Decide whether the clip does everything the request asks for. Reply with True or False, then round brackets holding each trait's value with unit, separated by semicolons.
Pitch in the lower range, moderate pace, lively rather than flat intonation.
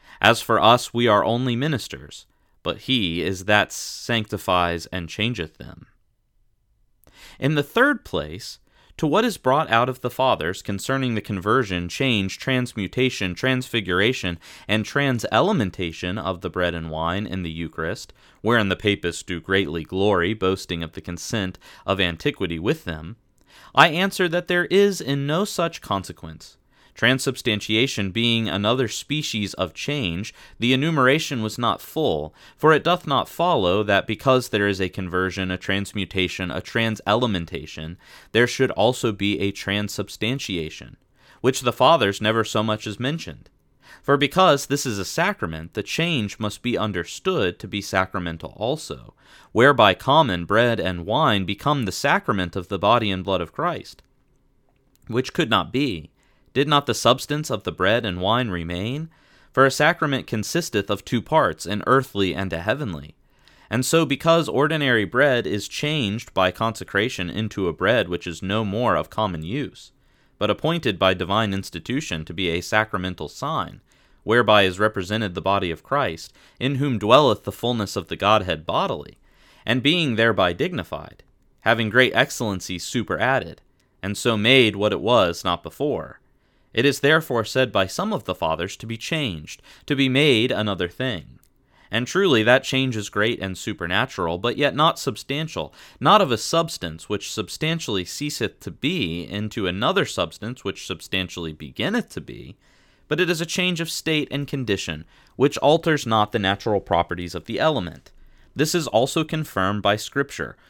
True (110 Hz; 160 wpm; 5.8 semitones)